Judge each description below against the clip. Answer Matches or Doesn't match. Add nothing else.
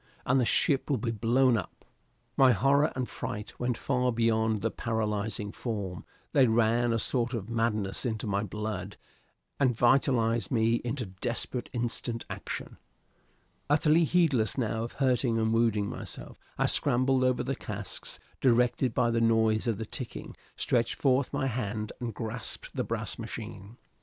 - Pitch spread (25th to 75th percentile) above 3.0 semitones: Doesn't match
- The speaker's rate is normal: Matches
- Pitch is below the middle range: Matches